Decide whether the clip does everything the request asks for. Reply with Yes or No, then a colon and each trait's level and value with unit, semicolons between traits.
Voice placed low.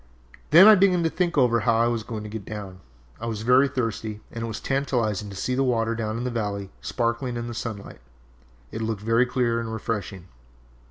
Yes: low, 115 Hz